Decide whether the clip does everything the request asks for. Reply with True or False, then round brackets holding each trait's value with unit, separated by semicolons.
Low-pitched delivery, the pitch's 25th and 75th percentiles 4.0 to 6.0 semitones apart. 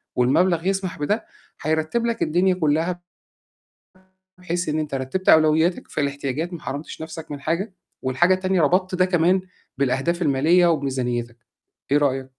False (160 Hz; 4.4 semitones)